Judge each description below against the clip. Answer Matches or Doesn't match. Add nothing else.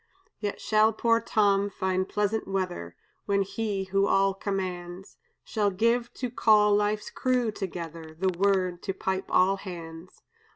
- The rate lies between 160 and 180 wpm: Doesn't match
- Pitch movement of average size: Doesn't match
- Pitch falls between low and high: Doesn't match